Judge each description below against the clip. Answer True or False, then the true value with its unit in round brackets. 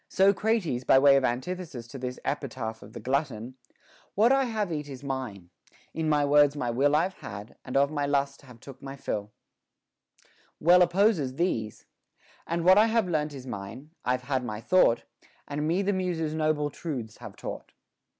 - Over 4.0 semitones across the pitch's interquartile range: True (5.2 semitones)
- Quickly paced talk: False (175 wpm)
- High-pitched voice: False (145 Hz)